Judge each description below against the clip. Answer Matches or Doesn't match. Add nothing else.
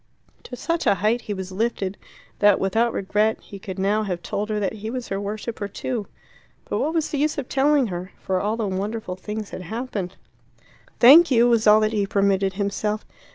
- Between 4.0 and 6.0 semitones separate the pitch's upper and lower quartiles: Doesn't match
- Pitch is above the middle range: Matches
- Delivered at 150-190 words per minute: Doesn't match